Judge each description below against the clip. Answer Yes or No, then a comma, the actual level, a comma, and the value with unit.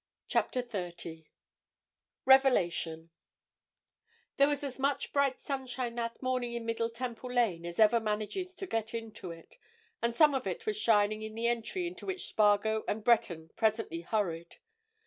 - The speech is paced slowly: No, average, 150 wpm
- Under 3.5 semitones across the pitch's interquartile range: No, average, 4.0 semitones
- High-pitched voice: Yes, high, 230 Hz